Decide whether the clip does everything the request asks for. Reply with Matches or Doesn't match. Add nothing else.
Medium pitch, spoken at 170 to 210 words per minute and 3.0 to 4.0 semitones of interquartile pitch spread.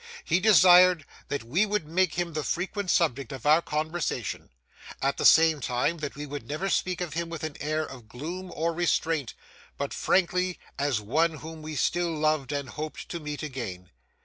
Matches